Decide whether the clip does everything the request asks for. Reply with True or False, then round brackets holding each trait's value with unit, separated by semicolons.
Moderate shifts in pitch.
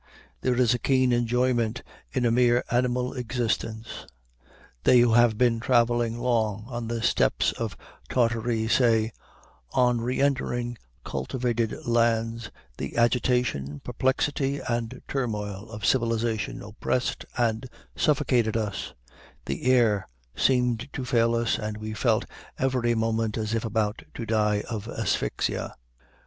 False (1.8 semitones)